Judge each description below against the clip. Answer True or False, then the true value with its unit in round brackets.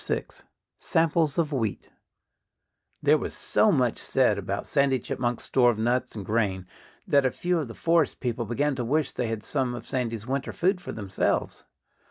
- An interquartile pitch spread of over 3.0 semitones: True (4.4 semitones)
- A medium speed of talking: True (180 wpm)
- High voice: False (125 Hz)